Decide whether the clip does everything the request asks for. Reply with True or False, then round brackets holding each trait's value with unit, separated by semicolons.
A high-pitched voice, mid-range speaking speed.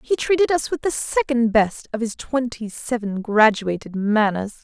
True (235 Hz; 170 wpm)